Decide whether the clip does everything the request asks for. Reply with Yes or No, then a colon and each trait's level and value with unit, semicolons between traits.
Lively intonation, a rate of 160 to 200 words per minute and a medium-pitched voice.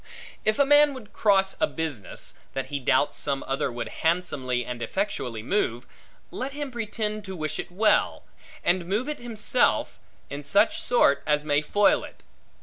Yes: wide, 7.5 semitones; average, 165 wpm; medium, 180 Hz